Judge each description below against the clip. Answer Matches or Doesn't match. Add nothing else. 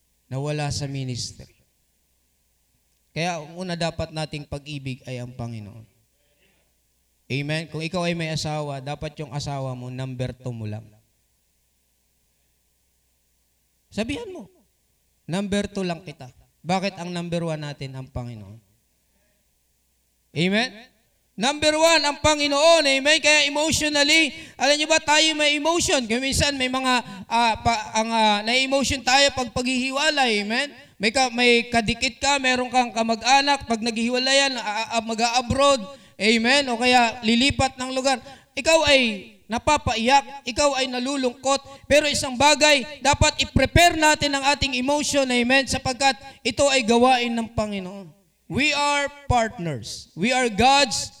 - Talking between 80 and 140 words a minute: Matches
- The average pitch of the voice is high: Matches